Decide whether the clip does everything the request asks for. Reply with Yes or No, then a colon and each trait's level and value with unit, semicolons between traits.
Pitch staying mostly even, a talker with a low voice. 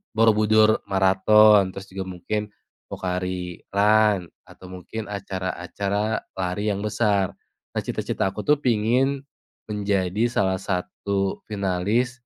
Yes: narrow, 2.3 semitones; low, 100 Hz